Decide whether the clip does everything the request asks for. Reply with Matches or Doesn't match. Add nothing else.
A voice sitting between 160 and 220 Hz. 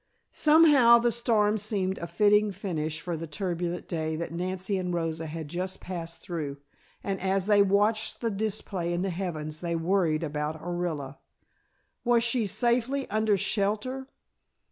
Matches